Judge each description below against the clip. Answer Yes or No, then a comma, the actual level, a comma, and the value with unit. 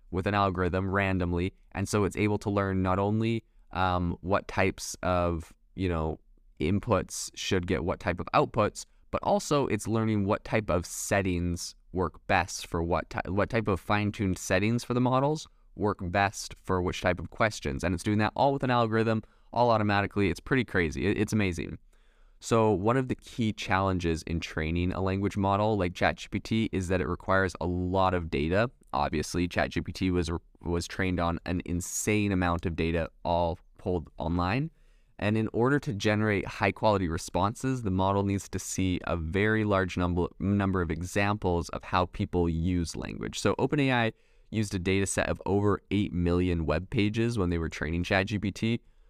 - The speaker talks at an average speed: Yes, average, 175 wpm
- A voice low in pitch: Yes, very low, 95 Hz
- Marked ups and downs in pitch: No, average, 3.3 semitones